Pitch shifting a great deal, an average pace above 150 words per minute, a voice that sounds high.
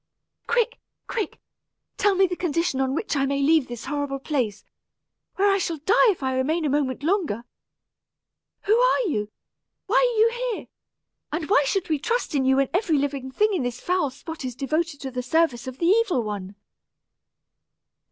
Yes: wide, 6.4 semitones; average, 180 wpm; very high, 300 Hz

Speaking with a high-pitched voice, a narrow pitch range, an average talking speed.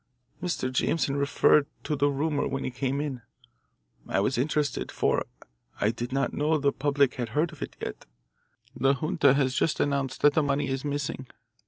No: medium, 140 Hz; narrow, 1.8 semitones; average, 180 wpm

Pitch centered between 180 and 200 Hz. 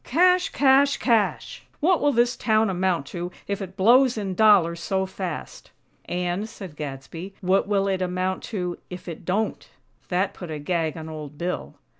Yes: high, 190 Hz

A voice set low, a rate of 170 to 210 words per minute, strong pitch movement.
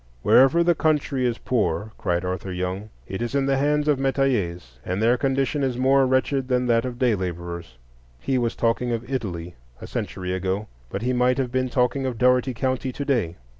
Yes: low, 125 Hz; average, 200 wpm; wide, 5.9 semitones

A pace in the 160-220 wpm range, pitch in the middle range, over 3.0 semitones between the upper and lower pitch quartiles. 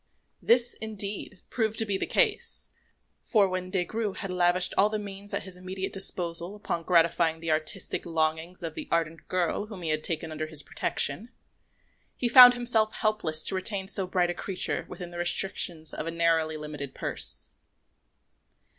Yes: average, 170 wpm; medium, 180 Hz; average, 3.7 semitones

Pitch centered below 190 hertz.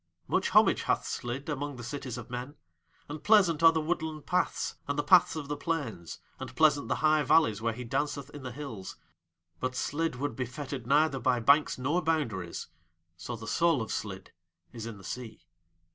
Yes: medium, 140 Hz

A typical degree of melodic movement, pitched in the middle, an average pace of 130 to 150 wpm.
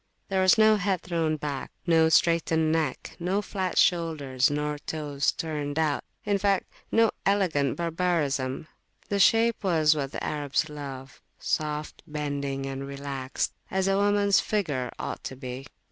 Yes: average, 4.8 semitones; medium, 155 Hz; average, 145 wpm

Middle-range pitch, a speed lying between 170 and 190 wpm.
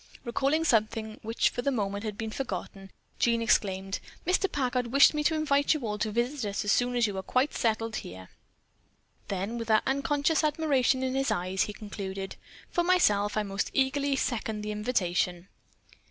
No: high, 230 Hz; average, 180 wpm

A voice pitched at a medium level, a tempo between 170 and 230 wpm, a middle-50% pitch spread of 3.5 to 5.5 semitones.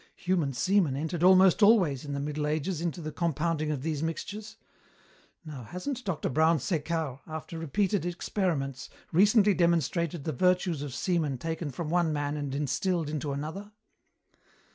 No: medium, 160 Hz; average, 150 wpm; average, 3.8 semitones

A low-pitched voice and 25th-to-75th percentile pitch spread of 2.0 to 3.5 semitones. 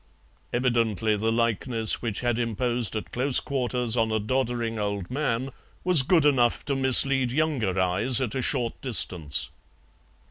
Yes: low, 120 Hz; average, 3.1 semitones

